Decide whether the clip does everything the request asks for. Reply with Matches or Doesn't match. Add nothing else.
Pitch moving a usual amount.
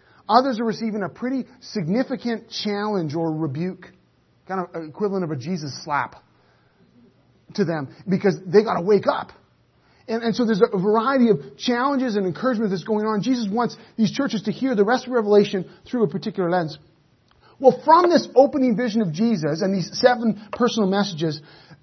Matches